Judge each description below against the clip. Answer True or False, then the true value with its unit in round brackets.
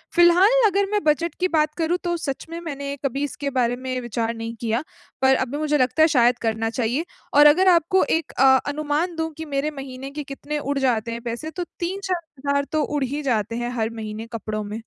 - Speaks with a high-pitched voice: True (280 Hz)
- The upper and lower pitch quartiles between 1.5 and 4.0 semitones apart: False (5.1 semitones)